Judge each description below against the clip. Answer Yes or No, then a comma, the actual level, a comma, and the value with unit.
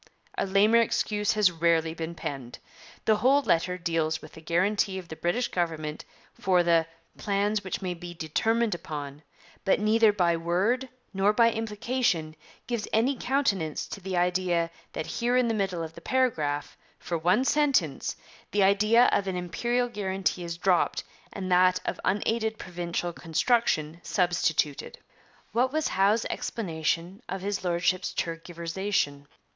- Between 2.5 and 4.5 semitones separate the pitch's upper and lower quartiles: Yes, average, 4.2 semitones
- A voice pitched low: No, medium, 185 Hz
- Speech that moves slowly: No, average, 150 wpm